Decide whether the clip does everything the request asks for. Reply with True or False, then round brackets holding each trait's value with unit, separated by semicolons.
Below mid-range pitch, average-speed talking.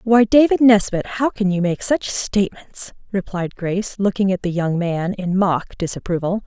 False (195 Hz; 175 wpm)